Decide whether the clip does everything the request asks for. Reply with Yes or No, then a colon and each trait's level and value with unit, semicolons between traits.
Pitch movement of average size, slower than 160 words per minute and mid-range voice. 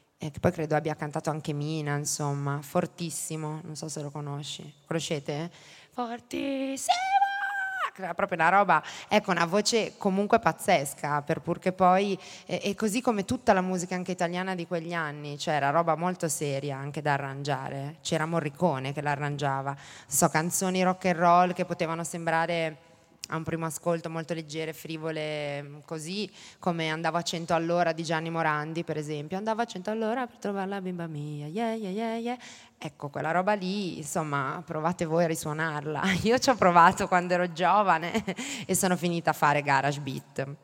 No: average, 3.5 semitones; average, 165 wpm; medium, 170 Hz